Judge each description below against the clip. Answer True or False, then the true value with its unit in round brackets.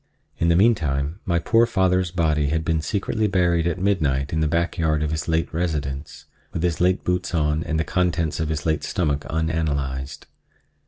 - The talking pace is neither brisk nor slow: True (190 wpm)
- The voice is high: False (80 Hz)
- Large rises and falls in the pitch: False (2.8 semitones)